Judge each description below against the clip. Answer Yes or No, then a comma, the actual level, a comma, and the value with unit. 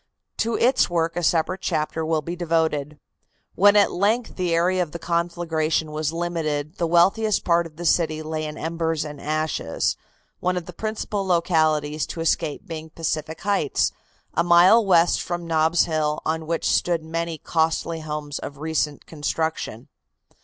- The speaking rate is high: No, average, 160 wpm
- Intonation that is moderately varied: No, narrow, 1.9 semitones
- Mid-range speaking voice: Yes, medium, 165 Hz